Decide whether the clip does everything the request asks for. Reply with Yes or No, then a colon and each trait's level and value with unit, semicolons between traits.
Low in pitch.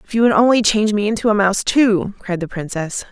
No: high, 205 Hz